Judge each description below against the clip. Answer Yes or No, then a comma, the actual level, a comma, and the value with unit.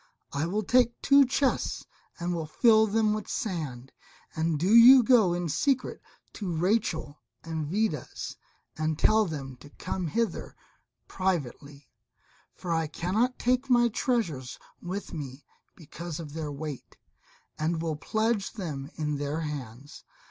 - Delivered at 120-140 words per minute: Yes, slow, 135 wpm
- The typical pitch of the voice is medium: Yes, medium, 170 Hz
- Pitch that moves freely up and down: Yes, wide, 6.5 semitones